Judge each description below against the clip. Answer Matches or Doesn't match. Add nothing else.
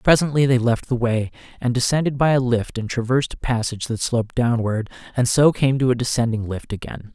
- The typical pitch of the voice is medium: Doesn't match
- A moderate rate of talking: Doesn't match